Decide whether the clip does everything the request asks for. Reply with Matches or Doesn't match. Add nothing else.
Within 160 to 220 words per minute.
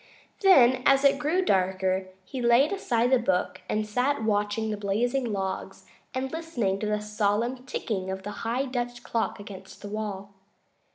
Matches